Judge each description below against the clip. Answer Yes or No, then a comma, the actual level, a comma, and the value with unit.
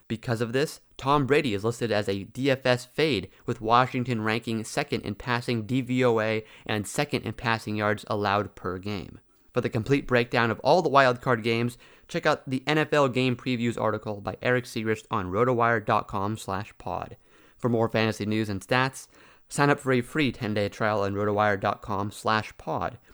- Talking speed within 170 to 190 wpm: No, average, 160 wpm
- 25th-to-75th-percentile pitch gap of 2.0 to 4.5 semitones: Yes, average, 3.2 semitones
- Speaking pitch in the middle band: No, low, 115 Hz